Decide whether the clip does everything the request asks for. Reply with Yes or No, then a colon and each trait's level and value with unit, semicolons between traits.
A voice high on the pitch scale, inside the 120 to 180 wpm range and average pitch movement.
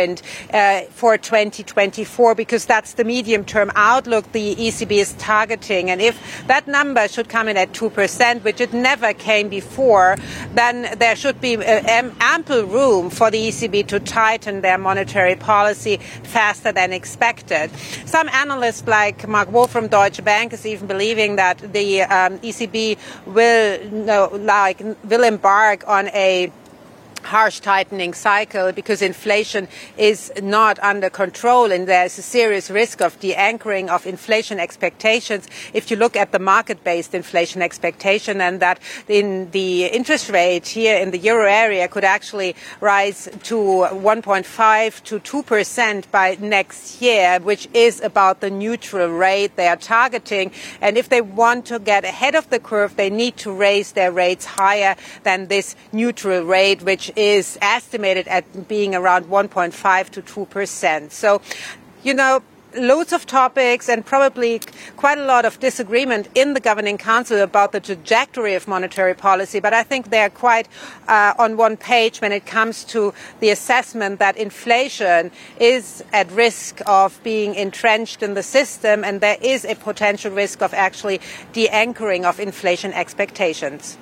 Yes: high, 210 Hz; average, 160 wpm; average, 3.0 semitones